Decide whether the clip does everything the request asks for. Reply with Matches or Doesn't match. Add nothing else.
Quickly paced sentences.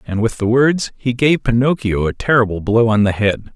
Matches